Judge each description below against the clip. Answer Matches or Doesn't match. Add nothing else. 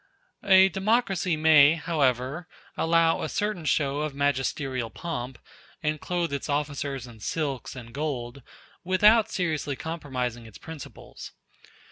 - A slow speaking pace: Matches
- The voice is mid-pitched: Matches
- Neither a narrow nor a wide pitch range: Matches